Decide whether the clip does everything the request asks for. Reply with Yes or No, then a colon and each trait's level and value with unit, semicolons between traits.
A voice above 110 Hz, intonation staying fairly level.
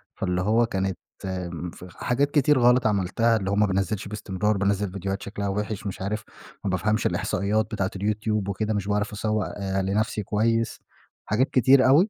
No: low, 105 Hz; narrow, 2.2 semitones